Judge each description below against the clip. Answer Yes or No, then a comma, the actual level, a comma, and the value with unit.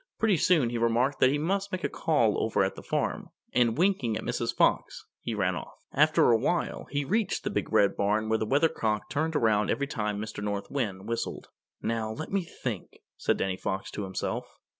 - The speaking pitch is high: No, low, 115 Hz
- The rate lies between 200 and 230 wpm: Yes, fast, 205 wpm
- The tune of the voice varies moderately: No, wide, 6.4 semitones